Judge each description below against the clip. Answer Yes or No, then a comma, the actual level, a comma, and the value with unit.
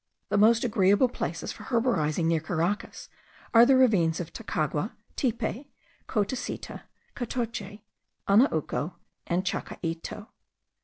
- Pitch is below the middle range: No, high, 205 Hz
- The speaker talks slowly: Yes, slow, 105 wpm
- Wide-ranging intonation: Yes, wide, 5.9 semitones